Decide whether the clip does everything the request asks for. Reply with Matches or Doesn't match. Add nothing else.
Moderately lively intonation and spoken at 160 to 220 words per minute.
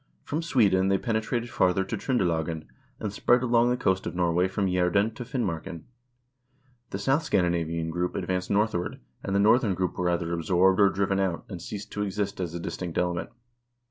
Matches